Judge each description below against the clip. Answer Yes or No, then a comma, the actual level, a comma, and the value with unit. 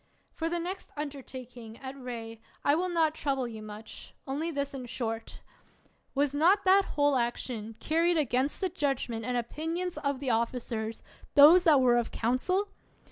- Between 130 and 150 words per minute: No, average, 165 wpm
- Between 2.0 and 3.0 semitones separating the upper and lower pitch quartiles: No, average, 5.2 semitones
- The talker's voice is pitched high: Yes, very high, 275 Hz